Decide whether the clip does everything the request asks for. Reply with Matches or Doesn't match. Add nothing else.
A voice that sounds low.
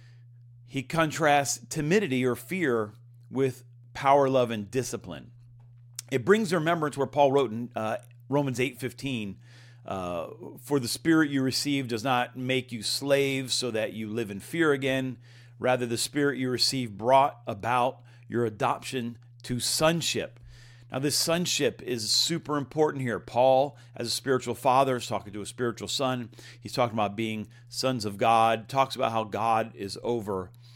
Matches